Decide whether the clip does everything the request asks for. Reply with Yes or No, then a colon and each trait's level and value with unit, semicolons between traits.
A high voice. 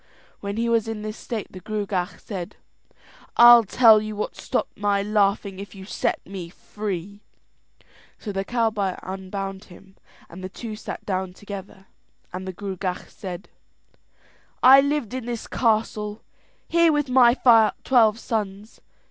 Yes: high, 205 Hz